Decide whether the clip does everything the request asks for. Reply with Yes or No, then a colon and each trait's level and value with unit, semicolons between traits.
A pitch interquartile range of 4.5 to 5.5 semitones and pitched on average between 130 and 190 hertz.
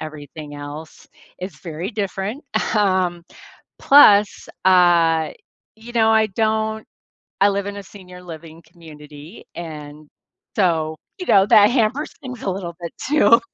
Yes: average, 5.0 semitones; medium, 185 Hz